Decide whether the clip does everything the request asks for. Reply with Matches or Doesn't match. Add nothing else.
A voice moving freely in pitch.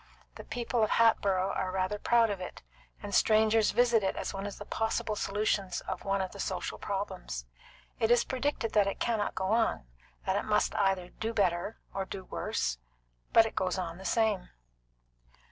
Doesn't match